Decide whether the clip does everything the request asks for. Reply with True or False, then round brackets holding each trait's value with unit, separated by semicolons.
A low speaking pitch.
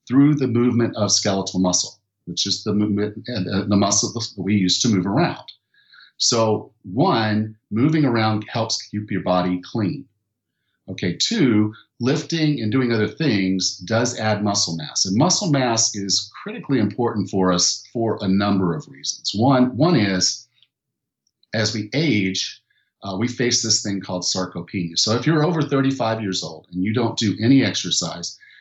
True (105 Hz)